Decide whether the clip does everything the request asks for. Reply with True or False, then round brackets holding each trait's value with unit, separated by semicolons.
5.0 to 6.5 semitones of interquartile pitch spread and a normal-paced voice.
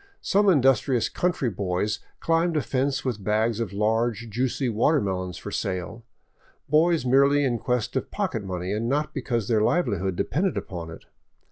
True (5.4 semitones; 155 wpm)